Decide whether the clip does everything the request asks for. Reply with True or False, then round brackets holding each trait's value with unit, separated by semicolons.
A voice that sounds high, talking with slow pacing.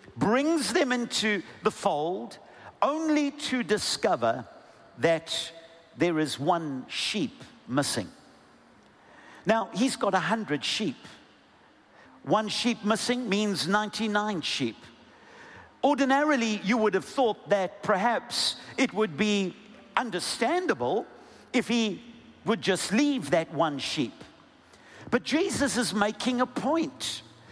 True (220 Hz; 110 wpm)